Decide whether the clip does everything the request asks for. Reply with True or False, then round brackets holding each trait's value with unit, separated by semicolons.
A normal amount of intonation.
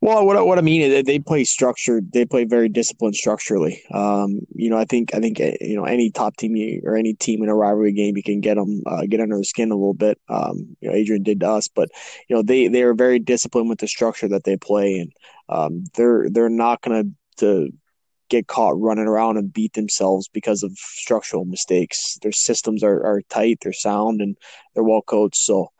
False (2.3 semitones)